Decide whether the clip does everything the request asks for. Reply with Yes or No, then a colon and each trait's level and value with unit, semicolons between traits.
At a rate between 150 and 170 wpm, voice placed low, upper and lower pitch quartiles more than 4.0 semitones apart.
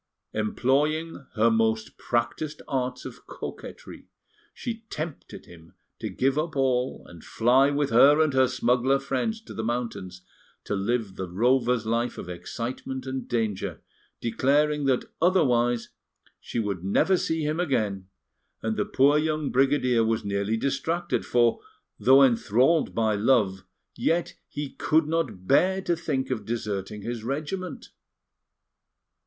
No: slow, 135 wpm; low, 125 Hz; average, 4.7 semitones